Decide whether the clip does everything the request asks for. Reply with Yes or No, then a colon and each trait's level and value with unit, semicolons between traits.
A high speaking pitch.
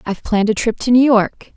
Yes: high, 225 Hz